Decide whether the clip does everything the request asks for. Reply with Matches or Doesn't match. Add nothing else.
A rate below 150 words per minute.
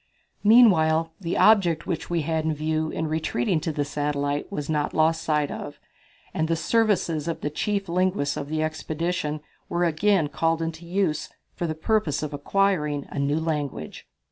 Doesn't match